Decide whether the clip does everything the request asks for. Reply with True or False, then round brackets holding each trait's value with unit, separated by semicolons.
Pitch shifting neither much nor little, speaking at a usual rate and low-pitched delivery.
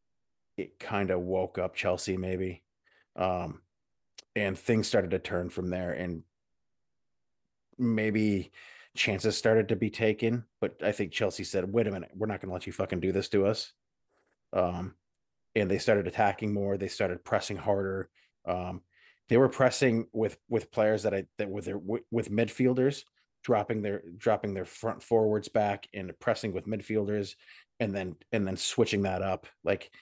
True (3.1 semitones; 170 wpm; 100 Hz)